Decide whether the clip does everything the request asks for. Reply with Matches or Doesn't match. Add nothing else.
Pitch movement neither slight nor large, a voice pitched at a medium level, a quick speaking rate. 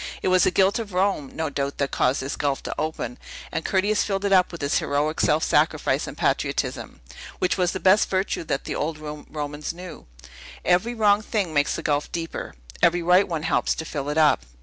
Matches